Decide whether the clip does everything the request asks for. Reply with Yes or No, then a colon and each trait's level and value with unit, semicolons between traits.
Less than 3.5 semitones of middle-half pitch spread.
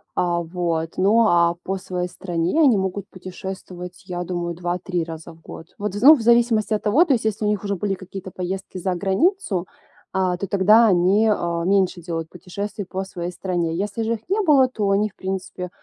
Yes: average, 3.0 semitones